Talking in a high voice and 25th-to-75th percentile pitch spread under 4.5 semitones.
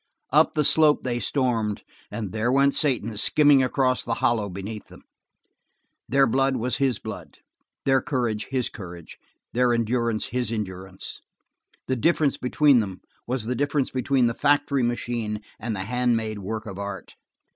No: low, 120 Hz; average, 3.7 semitones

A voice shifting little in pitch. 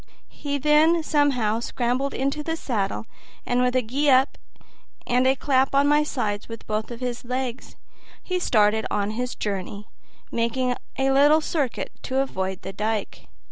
No: average, 4.2 semitones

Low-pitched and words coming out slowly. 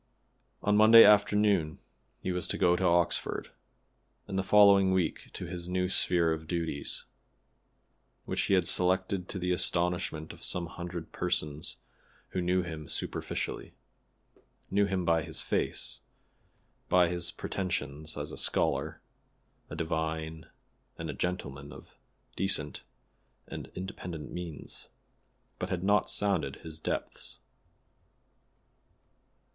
Yes: very low, 90 Hz; slow, 125 wpm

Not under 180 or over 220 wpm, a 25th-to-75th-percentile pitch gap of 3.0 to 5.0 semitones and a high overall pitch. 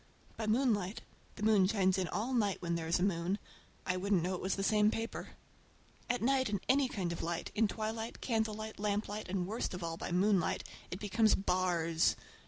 Yes: average, 190 wpm; average, 3.3 semitones; high, 200 Hz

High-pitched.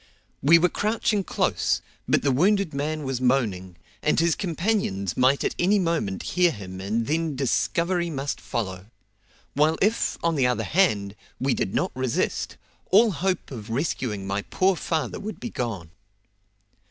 No: medium, 145 Hz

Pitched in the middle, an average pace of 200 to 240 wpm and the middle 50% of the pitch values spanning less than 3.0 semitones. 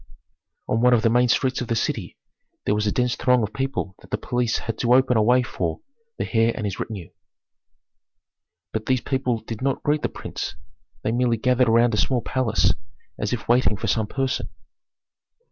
No: low, 120 Hz; fast, 205 wpm; narrow, 2.4 semitones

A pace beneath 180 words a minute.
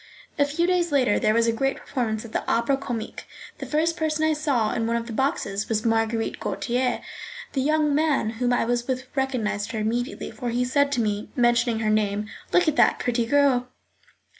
No: fast, 205 wpm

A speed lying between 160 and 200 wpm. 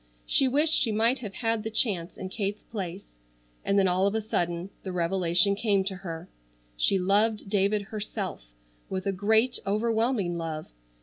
Yes: average, 170 wpm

